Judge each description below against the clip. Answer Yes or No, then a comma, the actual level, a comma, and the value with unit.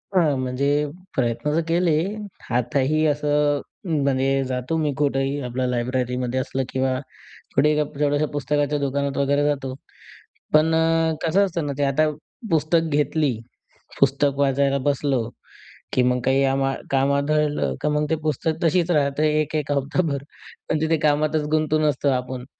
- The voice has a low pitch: No, medium, 145 Hz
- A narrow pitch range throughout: Yes, narrow, 2.2 semitones